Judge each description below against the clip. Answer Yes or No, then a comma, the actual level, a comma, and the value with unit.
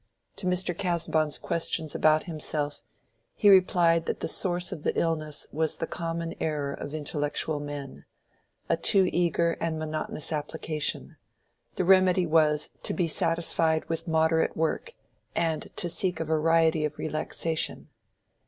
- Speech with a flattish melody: Yes, narrow, 1.7 semitones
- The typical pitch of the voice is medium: Yes, medium, 160 Hz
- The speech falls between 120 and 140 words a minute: Yes, slow, 135 wpm